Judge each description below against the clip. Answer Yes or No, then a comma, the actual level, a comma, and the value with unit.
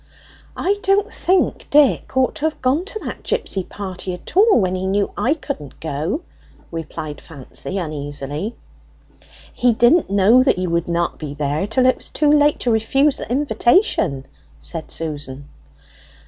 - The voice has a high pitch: Yes, high, 200 Hz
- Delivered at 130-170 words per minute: Yes, average, 160 wpm